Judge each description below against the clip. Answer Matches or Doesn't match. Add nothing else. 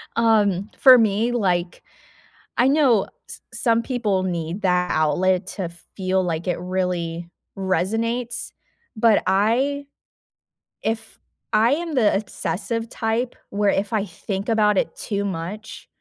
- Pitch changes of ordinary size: Matches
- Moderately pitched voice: Doesn't match